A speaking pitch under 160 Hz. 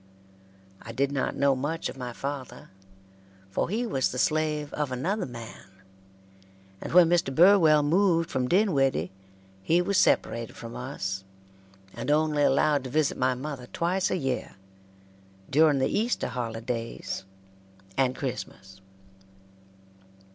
Yes: medium, 140 Hz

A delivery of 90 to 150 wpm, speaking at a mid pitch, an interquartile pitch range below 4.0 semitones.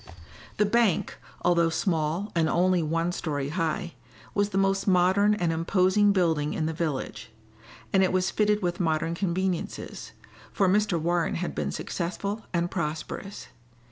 Yes: average, 145 wpm; medium, 175 Hz; average, 3.0 semitones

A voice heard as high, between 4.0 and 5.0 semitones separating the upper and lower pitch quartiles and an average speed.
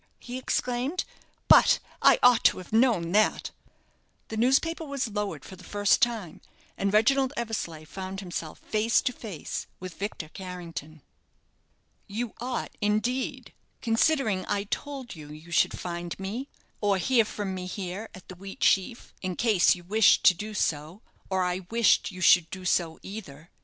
Yes: high, 200 Hz; average, 4.5 semitones; average, 155 wpm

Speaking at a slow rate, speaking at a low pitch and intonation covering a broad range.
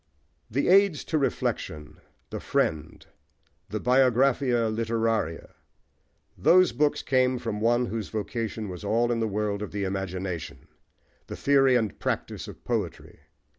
No: slow, 130 wpm; low, 115 Hz; average, 3.9 semitones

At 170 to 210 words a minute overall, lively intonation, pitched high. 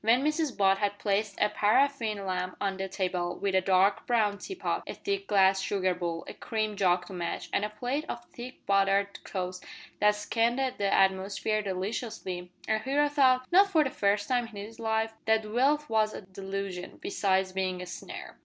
No: average, 190 wpm; average, 3.7 semitones; high, 205 Hz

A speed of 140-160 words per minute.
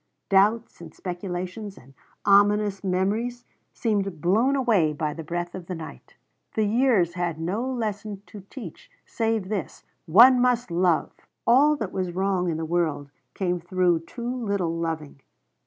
Yes: average, 150 wpm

